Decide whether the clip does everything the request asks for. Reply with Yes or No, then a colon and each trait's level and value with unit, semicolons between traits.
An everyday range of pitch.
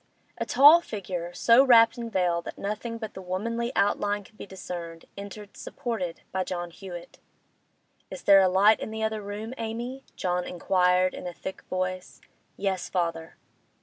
Yes: average, 3.5 semitones